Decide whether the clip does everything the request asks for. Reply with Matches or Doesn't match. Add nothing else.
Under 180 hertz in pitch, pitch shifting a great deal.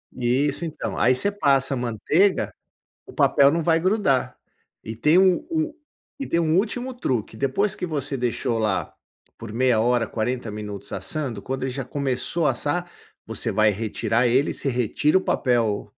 Matches